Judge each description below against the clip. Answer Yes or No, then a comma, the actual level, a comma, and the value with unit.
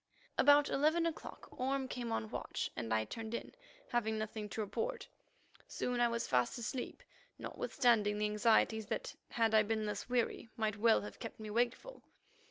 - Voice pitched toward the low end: No, high, 225 Hz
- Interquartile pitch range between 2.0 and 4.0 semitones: Yes, average, 2.7 semitones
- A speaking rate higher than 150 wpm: Yes, average, 170 wpm